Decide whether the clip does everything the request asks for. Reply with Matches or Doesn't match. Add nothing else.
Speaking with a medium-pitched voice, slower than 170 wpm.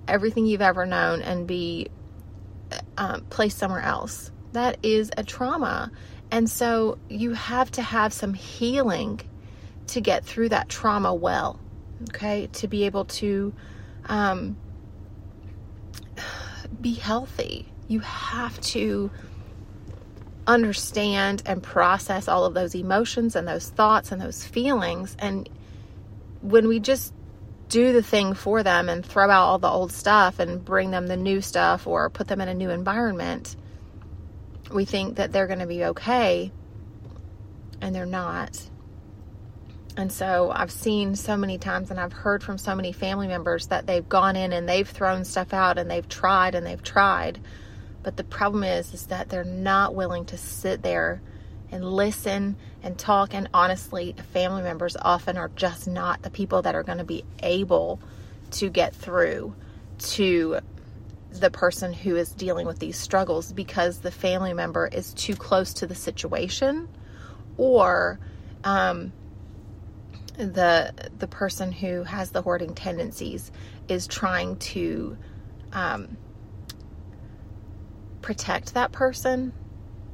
Matches